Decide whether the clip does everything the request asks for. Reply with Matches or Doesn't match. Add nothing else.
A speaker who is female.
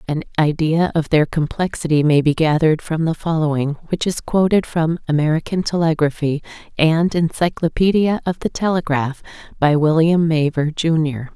Matches